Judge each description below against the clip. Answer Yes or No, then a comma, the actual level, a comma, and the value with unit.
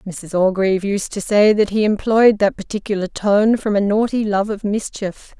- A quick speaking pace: No, average, 190 wpm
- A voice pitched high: Yes, high, 205 Hz